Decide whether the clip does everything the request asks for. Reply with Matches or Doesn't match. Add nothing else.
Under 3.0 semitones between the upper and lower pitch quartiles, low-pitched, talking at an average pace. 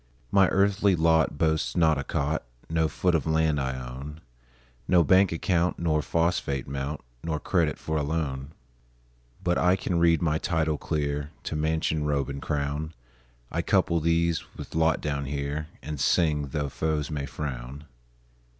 Matches